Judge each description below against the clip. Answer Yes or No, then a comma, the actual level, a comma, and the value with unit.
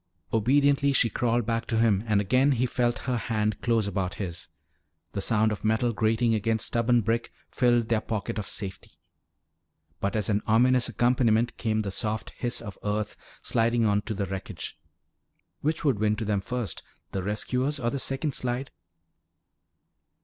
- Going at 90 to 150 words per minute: No, average, 165 wpm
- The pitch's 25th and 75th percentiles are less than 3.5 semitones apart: Yes, narrow, 2.6 semitones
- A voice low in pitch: Yes, low, 115 Hz